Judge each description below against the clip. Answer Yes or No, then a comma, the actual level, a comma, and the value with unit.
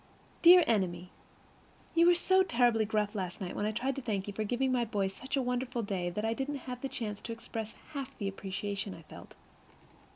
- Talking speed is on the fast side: Yes, fast, 220 wpm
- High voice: Yes, high, 225 Hz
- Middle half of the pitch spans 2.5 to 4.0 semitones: No, average, 4.5 semitones